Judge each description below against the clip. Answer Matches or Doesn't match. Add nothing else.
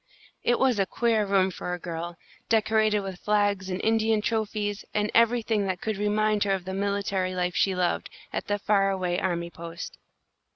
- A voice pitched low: Doesn't match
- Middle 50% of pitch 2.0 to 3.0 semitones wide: Matches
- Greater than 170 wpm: Matches